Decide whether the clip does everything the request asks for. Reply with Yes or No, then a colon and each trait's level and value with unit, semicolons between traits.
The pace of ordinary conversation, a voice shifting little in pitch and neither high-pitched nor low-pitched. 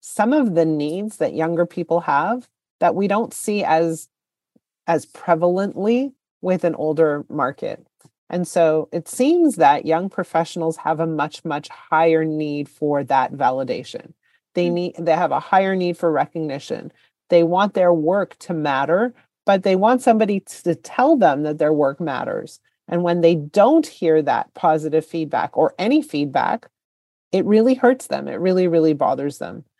No: average, 165 wpm; average, 3.6 semitones; medium, 170 Hz